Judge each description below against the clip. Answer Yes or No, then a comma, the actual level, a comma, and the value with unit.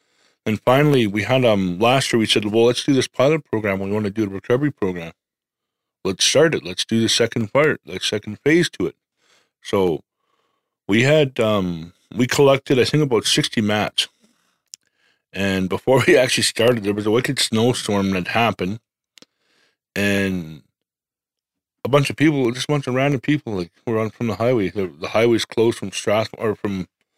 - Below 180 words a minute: No, average, 185 wpm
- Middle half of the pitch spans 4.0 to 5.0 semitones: Yes, average, 4.3 semitones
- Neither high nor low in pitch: No, low, 110 Hz